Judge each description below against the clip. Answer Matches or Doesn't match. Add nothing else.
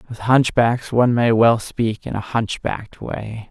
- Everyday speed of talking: Matches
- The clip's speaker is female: Doesn't match